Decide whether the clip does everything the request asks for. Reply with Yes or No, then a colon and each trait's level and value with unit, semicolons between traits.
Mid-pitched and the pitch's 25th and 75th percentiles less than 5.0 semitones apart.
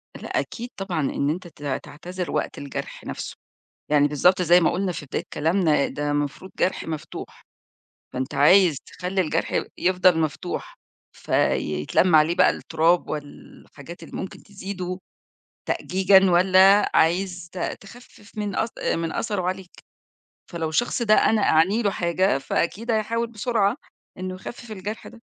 Yes: medium, 180 Hz; average, 3.7 semitones